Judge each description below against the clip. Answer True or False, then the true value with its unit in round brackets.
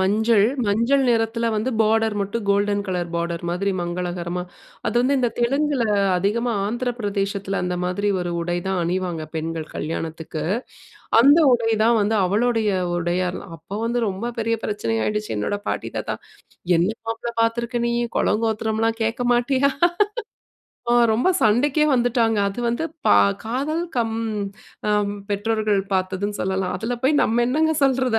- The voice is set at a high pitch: True (215 Hz)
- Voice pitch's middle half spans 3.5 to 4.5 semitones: True (4.0 semitones)